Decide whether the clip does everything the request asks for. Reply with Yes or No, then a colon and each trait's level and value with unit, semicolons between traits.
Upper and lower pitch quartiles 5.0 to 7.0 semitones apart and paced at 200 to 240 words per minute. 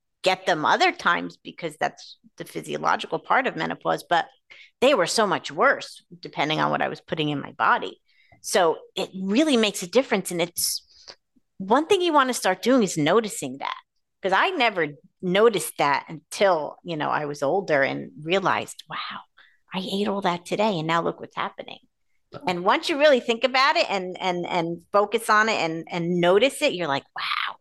No: average, 5.3 semitones; average, 190 wpm